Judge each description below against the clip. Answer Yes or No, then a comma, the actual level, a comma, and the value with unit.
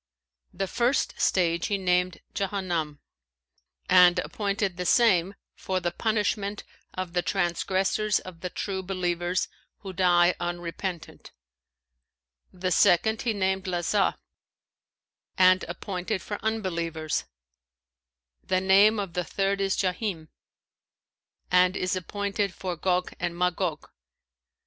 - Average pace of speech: No, slow, 110 wpm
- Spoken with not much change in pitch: Yes, narrow, 2.1 semitones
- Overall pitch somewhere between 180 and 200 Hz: Yes, medium, 185 Hz